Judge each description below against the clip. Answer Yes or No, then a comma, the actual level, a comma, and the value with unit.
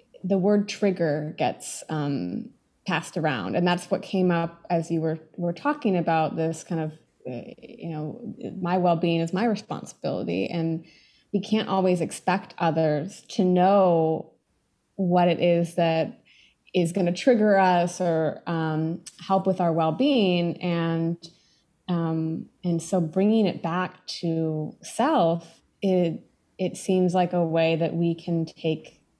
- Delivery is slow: No, average, 150 wpm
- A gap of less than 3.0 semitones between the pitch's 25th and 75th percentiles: Yes, narrow, 2.4 semitones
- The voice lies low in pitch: No, medium, 175 Hz